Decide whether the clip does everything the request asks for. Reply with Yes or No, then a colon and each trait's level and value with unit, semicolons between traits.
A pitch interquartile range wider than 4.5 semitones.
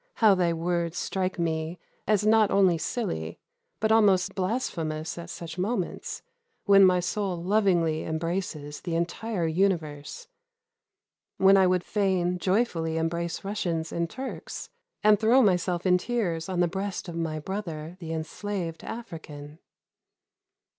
No: average, 3.3 semitones